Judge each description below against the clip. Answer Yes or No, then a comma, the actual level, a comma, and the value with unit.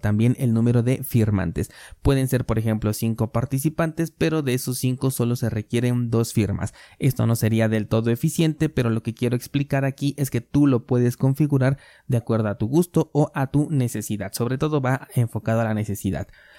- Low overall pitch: Yes, low, 120 Hz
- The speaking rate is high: Yes, fast, 195 wpm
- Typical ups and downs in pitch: Yes, average, 3.5 semitones